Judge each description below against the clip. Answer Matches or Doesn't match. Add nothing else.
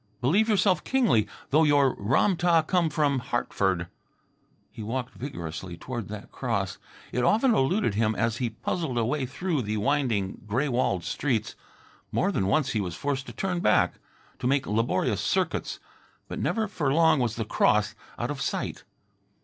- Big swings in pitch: Matches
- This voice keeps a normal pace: Matches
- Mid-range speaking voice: Doesn't match